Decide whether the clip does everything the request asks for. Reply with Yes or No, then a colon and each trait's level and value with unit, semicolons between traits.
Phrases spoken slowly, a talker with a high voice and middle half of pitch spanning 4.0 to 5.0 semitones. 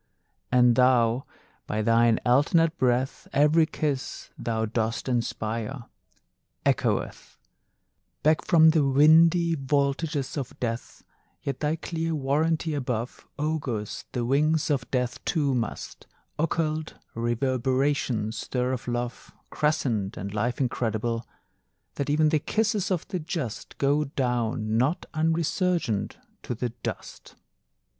No: slow, 115 wpm; low, 135 Hz; average, 4.6 semitones